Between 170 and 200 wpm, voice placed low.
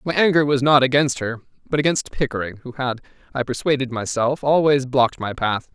Yes: average, 190 wpm; low, 130 Hz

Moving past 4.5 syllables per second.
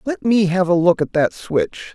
No: 4.4 syllables/s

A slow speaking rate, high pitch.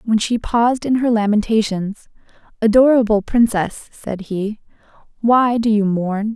Yes: slow, 130 wpm; high, 220 Hz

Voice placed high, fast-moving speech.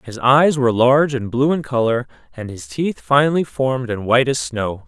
No: low, 130 Hz; fast, 210 wpm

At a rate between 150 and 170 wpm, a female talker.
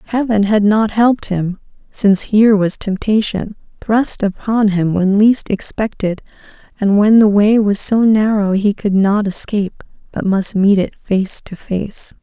Yes: average, 160 wpm; female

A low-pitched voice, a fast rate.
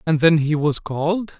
No: medium, 160 Hz; fast, 215 wpm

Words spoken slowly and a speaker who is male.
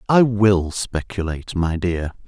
Yes: slow, 130 wpm; male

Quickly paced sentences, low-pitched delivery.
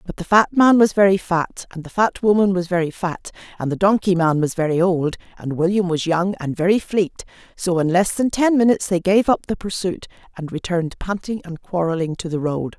No: fast, 220 wpm; medium, 185 Hz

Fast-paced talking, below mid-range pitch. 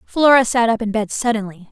No: fast, 210 wpm; high, 225 Hz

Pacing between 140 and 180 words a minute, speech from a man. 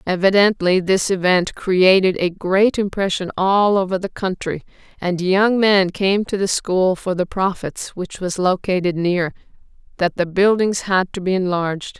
No: average, 160 wpm; female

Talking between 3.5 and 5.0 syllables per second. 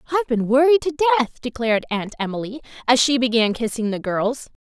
No: 6.0 syllables/s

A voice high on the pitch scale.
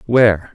No: low, 110 Hz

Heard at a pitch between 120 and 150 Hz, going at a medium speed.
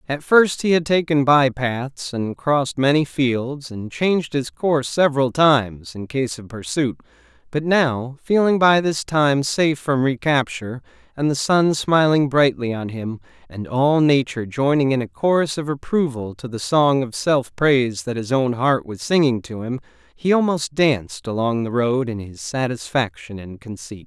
Yes: low, 135 Hz; average, 175 wpm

